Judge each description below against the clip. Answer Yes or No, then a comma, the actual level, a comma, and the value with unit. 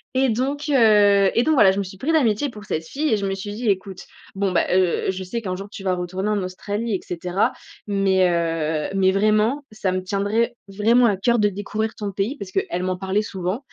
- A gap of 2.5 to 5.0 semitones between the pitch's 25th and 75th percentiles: Yes, average, 2.9 semitones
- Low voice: No, high, 200 Hz